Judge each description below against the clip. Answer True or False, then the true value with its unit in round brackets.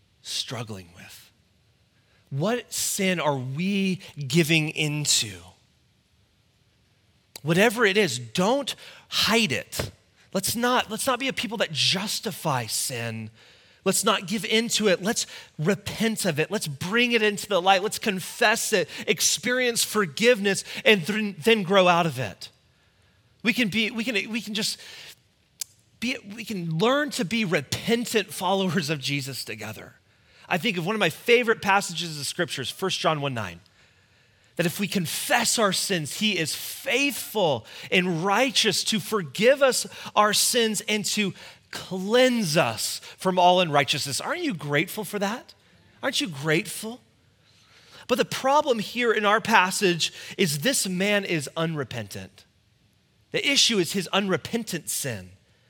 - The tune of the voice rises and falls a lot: True (7.9 semitones)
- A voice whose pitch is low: False (185 Hz)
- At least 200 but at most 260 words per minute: False (145 wpm)